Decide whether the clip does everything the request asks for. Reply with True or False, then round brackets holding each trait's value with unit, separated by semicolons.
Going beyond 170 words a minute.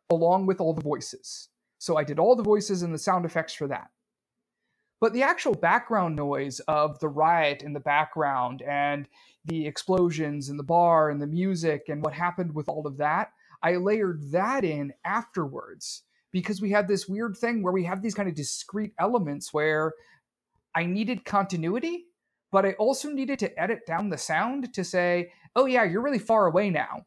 True (190 wpm)